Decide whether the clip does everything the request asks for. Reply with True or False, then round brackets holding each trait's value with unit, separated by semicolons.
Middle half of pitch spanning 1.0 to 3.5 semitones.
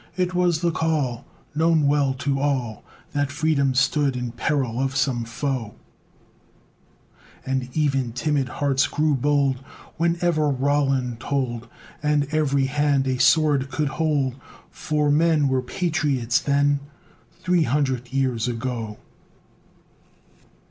True (2.7 semitones)